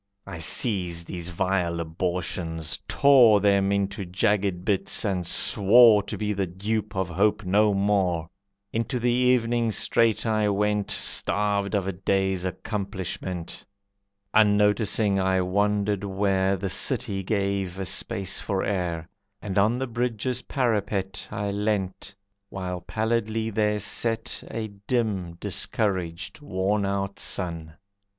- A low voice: Yes, low, 100 Hz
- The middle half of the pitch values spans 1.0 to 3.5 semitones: Yes, narrow, 2.4 semitones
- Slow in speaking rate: Yes, slow, 125 wpm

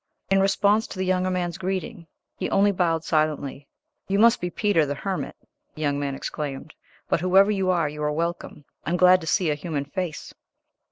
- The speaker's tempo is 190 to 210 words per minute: Yes, average, 200 wpm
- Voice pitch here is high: No, medium, 175 Hz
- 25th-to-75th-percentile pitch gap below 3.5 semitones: No, average, 4.0 semitones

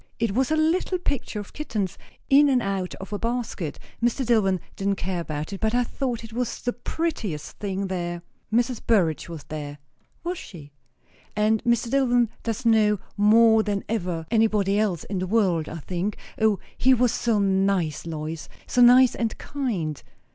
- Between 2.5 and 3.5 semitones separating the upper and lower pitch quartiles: No, average, 4.6 semitones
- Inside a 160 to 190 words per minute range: Yes, average, 175 wpm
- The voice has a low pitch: No, high, 210 Hz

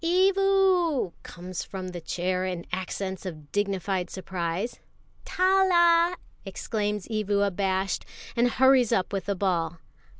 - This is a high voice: Yes, high, 200 Hz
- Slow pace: Yes, slow, 120 wpm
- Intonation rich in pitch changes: Yes, wide, 6.8 semitones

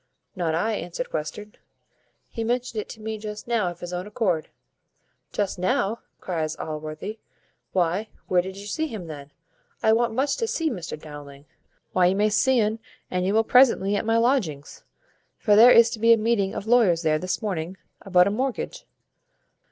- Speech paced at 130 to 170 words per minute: No, average, 185 wpm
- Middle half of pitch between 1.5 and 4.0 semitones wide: No, average, 4.5 semitones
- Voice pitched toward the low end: No, high, 205 Hz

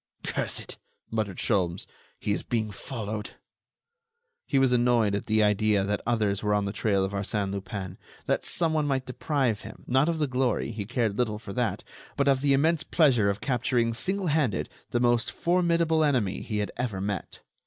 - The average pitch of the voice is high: No, low, 115 Hz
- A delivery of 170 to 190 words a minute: Yes, average, 175 wpm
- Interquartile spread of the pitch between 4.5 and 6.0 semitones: Yes, average, 4.8 semitones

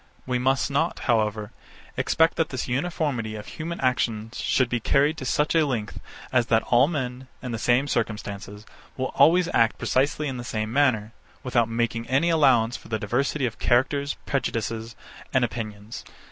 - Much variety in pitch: No, average, 3.7 semitones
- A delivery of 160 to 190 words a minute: Yes, average, 175 wpm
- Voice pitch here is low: Yes, low, 125 Hz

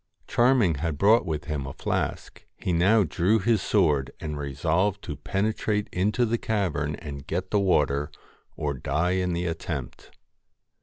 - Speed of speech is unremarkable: Yes, average, 155 wpm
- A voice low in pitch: Yes, very low, 90 Hz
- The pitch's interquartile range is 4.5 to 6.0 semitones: Yes, wide, 5.5 semitones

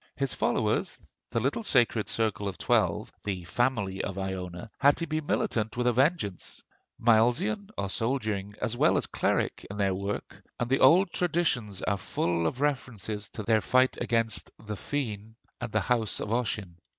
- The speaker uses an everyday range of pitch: Yes, average, 4.5 semitones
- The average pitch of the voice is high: No, low, 110 Hz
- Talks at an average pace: Yes, average, 170 wpm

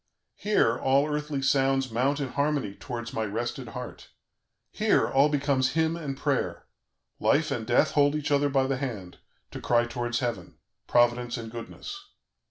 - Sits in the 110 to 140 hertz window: Yes, low, 135 Hz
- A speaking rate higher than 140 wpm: Yes, average, 160 wpm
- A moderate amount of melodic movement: Yes, average, 3.2 semitones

